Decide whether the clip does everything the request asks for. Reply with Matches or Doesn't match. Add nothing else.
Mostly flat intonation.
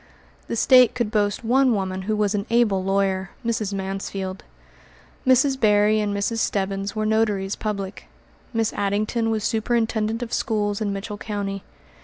Matches